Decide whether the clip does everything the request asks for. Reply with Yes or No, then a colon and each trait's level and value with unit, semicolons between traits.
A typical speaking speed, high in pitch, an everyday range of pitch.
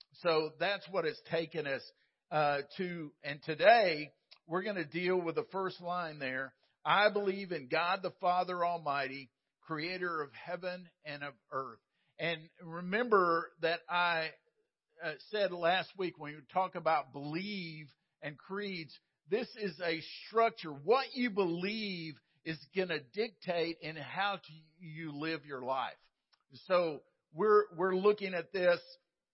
No: average, 145 wpm; medium, 170 Hz; average, 3.4 semitones